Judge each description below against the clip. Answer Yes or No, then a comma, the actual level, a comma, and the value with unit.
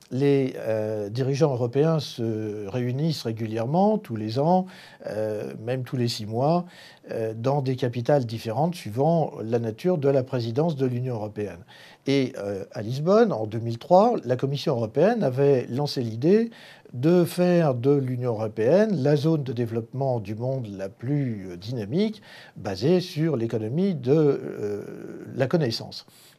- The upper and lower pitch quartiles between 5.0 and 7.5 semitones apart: Yes, average, 5.3 semitones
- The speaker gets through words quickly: No, slow, 145 wpm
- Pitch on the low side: Yes, low, 130 Hz